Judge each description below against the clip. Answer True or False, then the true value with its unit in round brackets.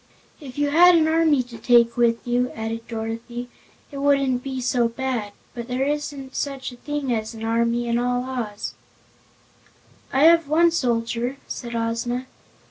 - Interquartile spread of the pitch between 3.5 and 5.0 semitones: False (3.1 semitones)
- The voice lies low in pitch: False (245 Hz)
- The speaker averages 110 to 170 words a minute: True (160 wpm)